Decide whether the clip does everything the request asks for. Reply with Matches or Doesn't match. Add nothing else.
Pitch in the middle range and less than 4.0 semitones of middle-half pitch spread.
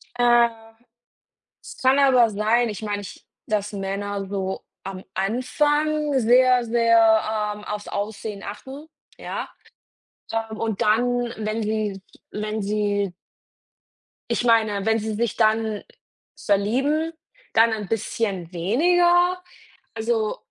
Doesn't match